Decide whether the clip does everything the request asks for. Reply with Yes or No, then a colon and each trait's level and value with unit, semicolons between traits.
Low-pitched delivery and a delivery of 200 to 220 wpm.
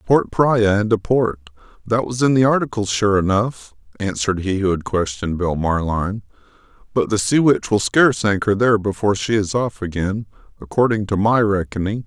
No: low, 105 Hz; average, 180 wpm